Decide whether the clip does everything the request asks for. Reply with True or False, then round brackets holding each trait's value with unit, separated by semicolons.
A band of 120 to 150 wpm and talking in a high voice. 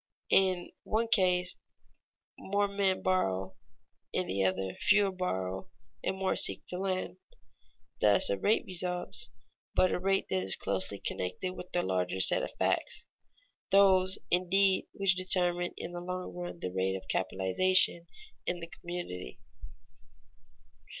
False (135 wpm; 180 Hz)